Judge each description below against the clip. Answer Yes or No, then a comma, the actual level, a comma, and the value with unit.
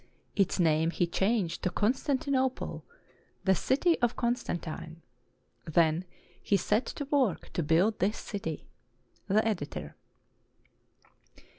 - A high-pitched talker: Yes, high, 195 Hz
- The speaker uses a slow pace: Yes, slow, 110 wpm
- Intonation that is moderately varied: No, wide, 6.1 semitones